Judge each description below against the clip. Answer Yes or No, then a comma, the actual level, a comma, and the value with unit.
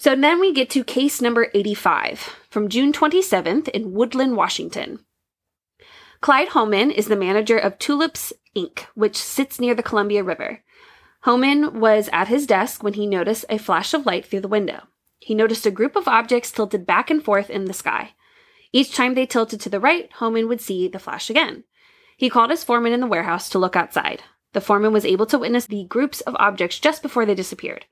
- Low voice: No, high, 235 Hz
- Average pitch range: No, wide, 5.7 semitones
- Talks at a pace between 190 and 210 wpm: Yes, average, 200 wpm